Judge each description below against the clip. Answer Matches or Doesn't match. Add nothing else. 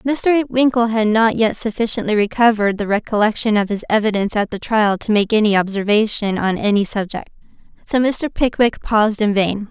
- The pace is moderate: Matches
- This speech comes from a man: Doesn't match